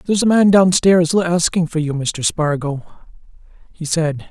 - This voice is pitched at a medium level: Yes, medium, 170 Hz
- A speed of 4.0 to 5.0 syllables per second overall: Yes, 4.5 syllables/s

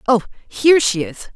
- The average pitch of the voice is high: Yes, high, 225 Hz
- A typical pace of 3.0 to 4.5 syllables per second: No, 5.2 syllables/s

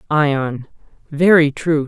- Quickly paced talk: No, slow, 95 wpm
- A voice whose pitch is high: No, medium, 150 Hz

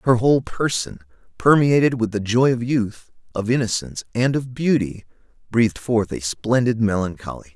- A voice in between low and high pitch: No, low, 115 Hz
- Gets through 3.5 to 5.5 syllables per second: Yes, 5.1 syllables/s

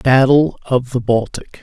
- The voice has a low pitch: Yes, low, 130 Hz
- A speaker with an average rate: Yes, average, 150 wpm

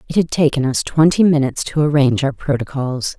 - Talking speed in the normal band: Yes, average, 190 wpm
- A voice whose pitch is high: No, medium, 145 Hz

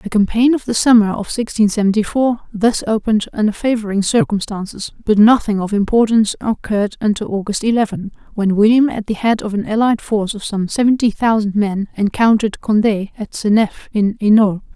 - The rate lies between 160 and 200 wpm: Yes, average, 170 wpm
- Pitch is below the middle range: No, high, 215 Hz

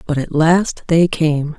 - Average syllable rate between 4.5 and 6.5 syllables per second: No, 3.6 syllables/s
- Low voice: No, medium, 160 Hz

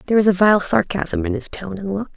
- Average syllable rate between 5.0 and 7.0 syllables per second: Yes, 6.1 syllables/s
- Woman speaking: Yes, female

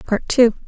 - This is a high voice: Yes, high, 225 Hz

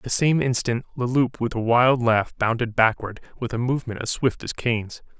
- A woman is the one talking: No, male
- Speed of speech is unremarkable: No, fast, 220 wpm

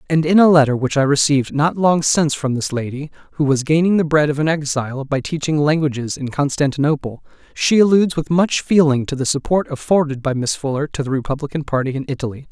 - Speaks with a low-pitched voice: No, medium, 145 Hz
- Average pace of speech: No, fast, 210 wpm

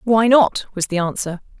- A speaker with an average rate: Yes, average, 190 wpm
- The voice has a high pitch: Yes, high, 205 Hz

